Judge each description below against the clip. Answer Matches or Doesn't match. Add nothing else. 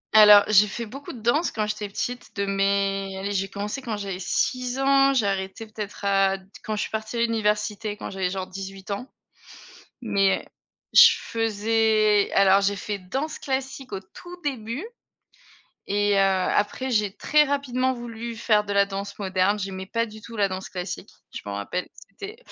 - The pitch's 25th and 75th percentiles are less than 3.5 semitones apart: Matches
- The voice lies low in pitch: Doesn't match